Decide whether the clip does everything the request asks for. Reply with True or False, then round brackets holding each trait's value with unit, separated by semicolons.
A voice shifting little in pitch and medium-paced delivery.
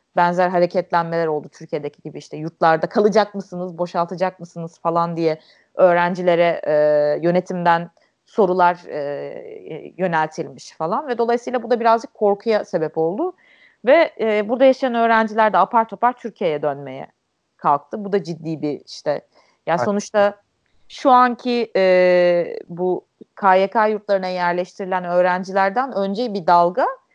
False (4.2 semitones; 125 wpm)